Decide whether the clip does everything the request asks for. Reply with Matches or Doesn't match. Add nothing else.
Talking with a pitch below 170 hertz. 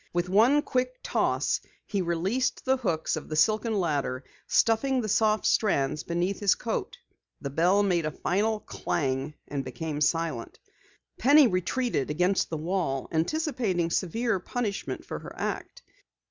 Doesn't match